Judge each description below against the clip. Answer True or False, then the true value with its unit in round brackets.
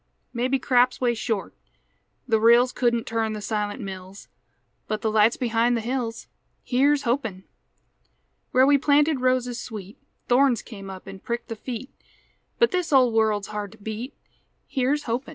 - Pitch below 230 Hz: False (235 Hz)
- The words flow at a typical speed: True (155 wpm)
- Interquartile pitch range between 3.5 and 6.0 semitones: False (3.1 semitones)